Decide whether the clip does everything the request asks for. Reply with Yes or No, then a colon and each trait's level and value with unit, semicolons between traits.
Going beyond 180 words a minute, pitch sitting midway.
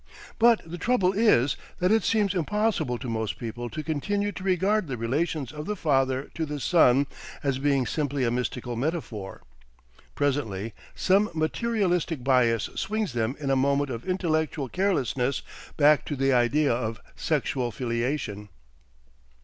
No: average, 150 wpm; medium, 145 Hz